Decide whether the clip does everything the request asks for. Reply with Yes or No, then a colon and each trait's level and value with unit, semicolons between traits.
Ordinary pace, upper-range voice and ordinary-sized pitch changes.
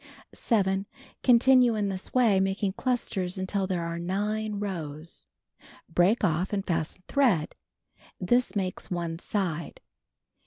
No: slow, 130 wpm; high, 195 Hz; average, 3.5 semitones